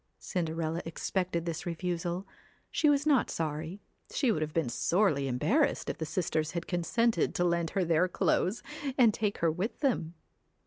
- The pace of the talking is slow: No, average, 165 wpm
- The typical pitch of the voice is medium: Yes, medium, 175 Hz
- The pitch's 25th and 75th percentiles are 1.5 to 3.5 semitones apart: No, average, 3.9 semitones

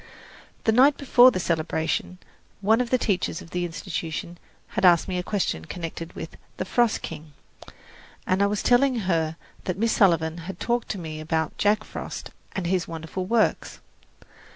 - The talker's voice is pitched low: No, medium, 185 Hz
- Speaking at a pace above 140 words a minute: Yes, average, 170 wpm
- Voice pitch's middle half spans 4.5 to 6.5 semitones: Yes, average, 4.9 semitones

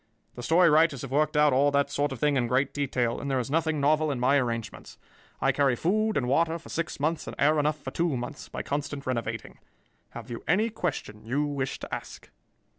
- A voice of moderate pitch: Yes, medium, 145 Hz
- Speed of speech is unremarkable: No, fast, 220 wpm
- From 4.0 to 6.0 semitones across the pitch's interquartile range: No, average, 3.3 semitones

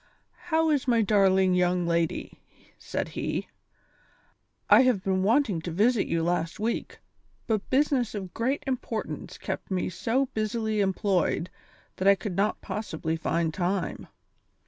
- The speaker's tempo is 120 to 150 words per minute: Yes, average, 140 wpm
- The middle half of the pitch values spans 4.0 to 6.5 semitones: Yes, average, 4.5 semitones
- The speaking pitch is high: Yes, high, 200 Hz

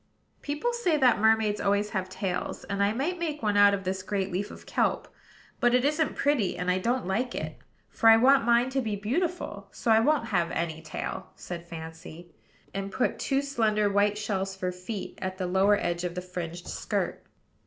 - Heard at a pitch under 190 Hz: No, high, 205 Hz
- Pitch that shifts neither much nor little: Yes, average, 4.7 semitones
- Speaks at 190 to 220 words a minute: Yes, average, 200 wpm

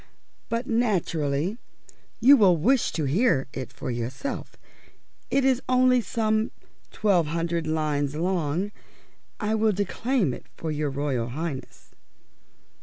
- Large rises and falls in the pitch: Yes, wide, 7.3 semitones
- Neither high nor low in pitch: Yes, medium, 175 Hz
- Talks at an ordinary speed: No, slow, 120 wpm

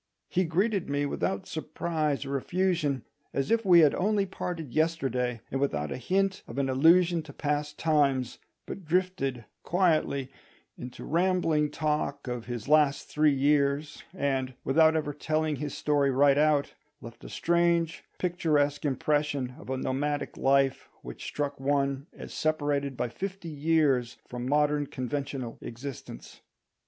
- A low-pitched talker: No, medium, 145 Hz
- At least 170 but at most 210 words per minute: No, average, 145 wpm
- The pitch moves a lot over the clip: No, average, 3.1 semitones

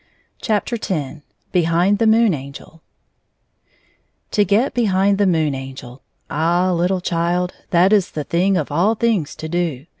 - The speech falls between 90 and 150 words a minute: Yes, average, 145 wpm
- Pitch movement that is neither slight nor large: Yes, average, 4.2 semitones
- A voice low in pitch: No, medium, 175 Hz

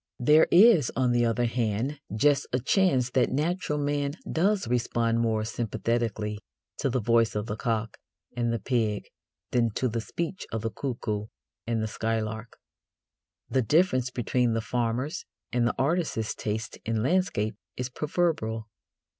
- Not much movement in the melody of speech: No, average, 3.9 semitones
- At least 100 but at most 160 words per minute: Yes, average, 150 wpm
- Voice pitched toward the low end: Yes, low, 120 Hz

